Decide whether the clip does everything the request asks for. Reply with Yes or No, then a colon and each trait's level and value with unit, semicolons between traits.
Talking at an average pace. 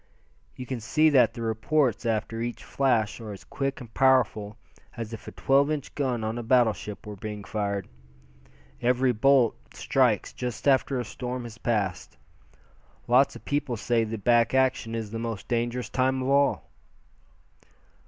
Yes: average, 165 wpm